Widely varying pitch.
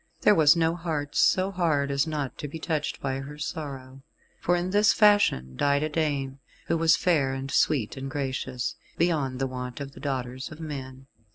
No: average, 3.4 semitones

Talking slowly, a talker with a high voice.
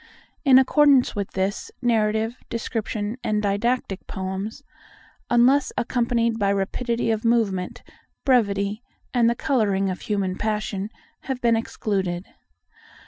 Yes: slow, 105 wpm; high, 220 Hz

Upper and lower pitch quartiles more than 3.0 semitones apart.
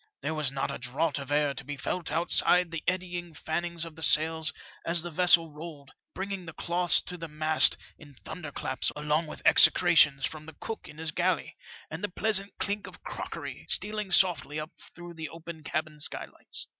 No: narrow, 2.6 semitones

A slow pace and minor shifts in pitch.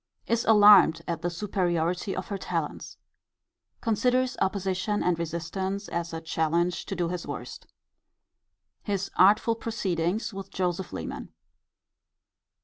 No: slow, 120 wpm; average, 3.3 semitones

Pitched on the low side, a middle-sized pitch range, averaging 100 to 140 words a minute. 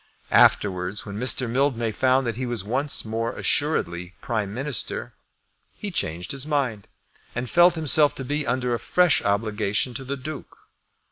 No: low, 125 Hz; average, 4.9 semitones; average, 155 wpm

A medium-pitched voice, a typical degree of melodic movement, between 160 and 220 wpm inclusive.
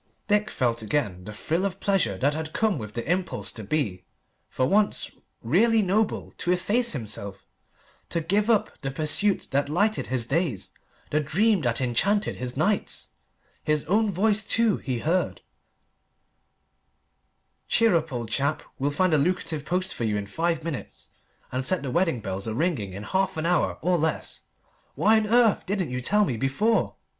No: medium, 160 Hz; wide, 7.8 semitones; average, 170 wpm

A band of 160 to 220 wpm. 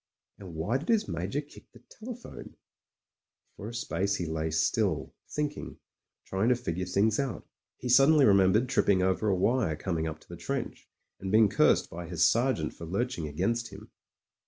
Yes: average, 175 wpm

